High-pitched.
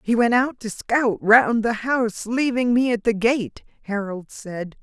Yes: high, 225 Hz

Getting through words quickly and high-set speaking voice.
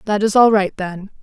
Yes: fast, 245 wpm; high, 205 Hz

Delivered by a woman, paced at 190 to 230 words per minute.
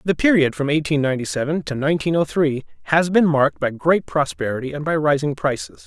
No: male; fast, 205 wpm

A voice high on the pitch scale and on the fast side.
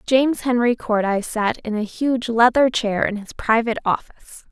No: high, 230 Hz; average, 175 wpm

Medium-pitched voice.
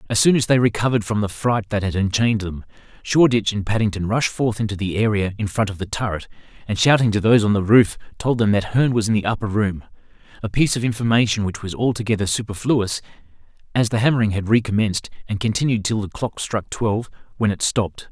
No: low, 110 Hz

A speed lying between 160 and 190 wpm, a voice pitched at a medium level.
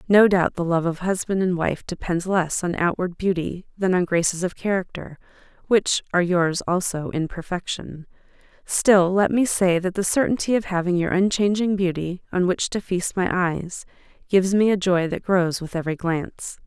Yes: average, 185 wpm; medium, 180 Hz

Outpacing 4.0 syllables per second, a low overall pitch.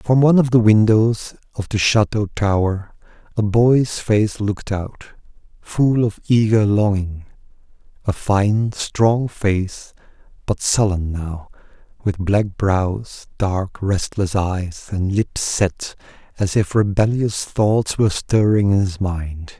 No: 3.5 syllables/s; low, 100 Hz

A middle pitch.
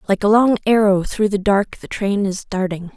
No: high, 200 Hz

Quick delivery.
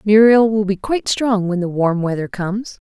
Yes: fast, 210 wpm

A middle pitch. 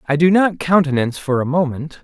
Yes: medium, 155 Hz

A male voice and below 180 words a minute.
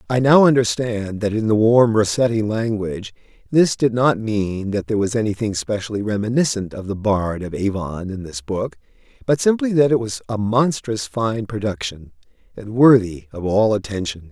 Yes: male; average, 170 wpm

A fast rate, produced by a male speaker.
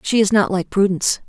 No: fast, 235 wpm; female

